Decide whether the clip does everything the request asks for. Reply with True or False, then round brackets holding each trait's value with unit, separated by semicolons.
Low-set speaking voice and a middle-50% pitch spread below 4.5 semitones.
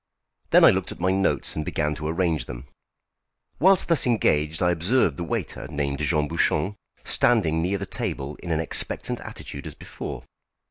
True (80 Hz; 4.0 semitones)